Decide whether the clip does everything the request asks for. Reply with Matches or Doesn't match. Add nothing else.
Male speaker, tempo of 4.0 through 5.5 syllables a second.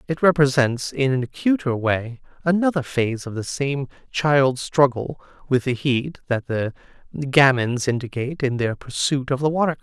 Matches